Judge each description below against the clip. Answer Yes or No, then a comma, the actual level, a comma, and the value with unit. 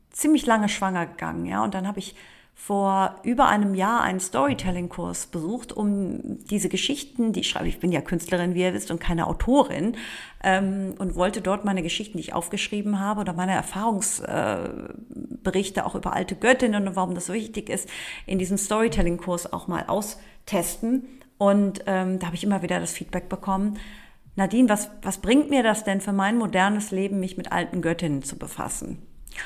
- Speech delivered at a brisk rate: No, average, 180 wpm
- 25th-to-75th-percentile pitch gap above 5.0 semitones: No, average, 2.8 semitones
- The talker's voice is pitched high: Yes, high, 195 Hz